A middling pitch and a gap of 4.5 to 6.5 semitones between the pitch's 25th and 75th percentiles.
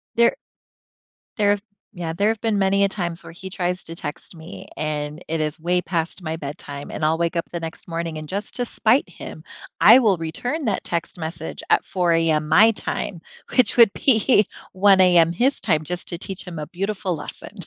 No: medium, 175 Hz; average, 3.9 semitones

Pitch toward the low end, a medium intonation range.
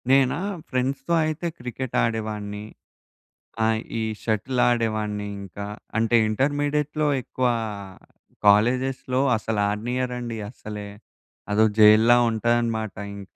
Yes: low, 115 Hz; average, 3.2 semitones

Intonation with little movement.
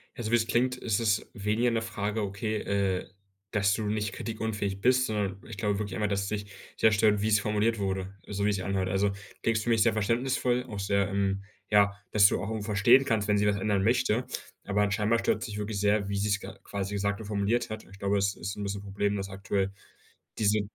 Yes: narrow, 1.8 semitones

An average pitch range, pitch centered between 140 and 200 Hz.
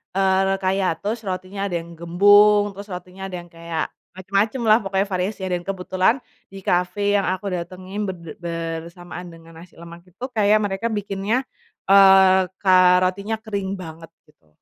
No: narrow, 2.3 semitones; high, 190 Hz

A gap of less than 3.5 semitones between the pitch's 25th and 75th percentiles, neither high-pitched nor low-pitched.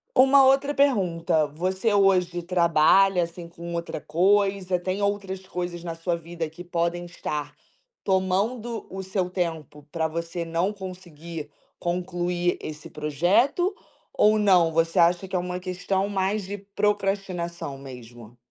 Yes: narrow, 2.6 semitones; medium, 180 Hz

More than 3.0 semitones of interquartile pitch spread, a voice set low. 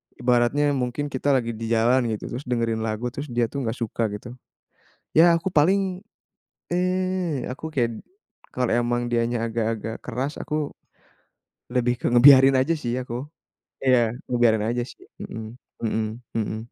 Yes: average, 3.6 semitones; low, 120 Hz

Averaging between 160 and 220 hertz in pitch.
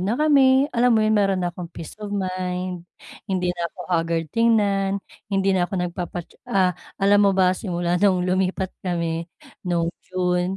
Yes: medium, 185 Hz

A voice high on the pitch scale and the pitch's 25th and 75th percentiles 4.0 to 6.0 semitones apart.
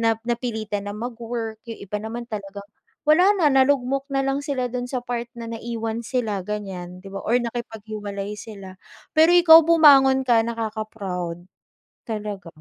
No: high, 230 Hz; average, 3.3 semitones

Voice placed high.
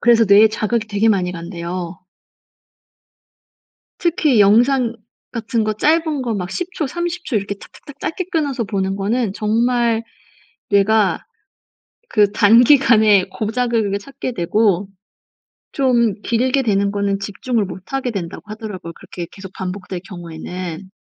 Yes: high, 215 Hz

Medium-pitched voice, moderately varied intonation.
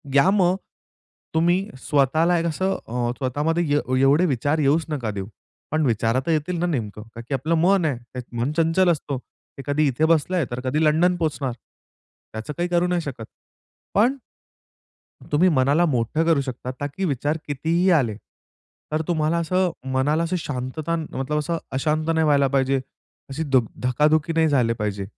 Yes: medium, 150 Hz; average, 4.2 semitones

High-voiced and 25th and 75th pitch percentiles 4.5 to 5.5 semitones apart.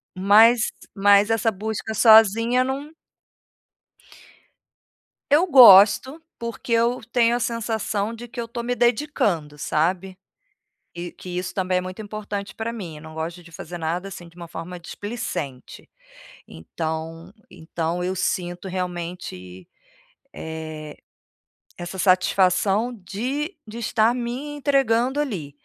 Yes: high, 200 Hz; average, 5.2 semitones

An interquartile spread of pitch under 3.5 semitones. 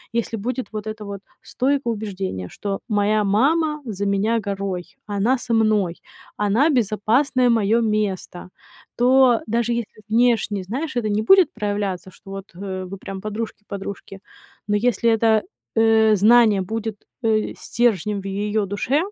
Yes: average, 2.9 semitones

